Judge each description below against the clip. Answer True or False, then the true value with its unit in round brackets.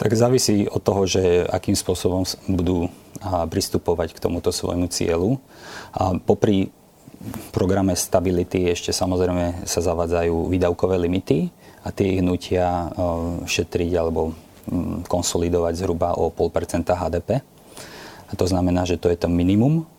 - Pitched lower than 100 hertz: True (90 Hz)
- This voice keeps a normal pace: True (125 wpm)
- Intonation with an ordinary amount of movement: False (2.3 semitones)